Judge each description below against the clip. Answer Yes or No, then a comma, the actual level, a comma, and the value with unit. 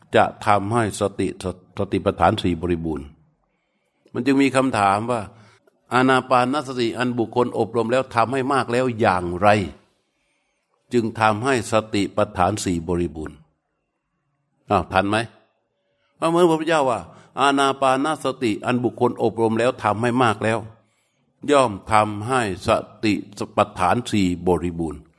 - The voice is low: Yes, low, 115 Hz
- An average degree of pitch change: Yes, average, 4.5 semitones